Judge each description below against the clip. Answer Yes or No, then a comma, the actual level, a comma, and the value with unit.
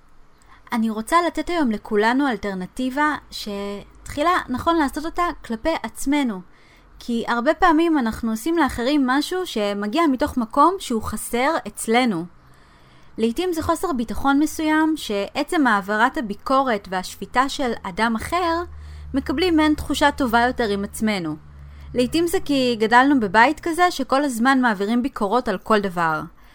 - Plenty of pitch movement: Yes, wide, 6.5 semitones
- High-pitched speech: Yes, very high, 250 Hz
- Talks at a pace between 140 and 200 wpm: No, average, 130 wpm